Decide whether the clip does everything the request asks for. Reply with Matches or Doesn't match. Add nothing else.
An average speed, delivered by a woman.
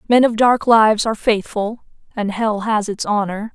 Matches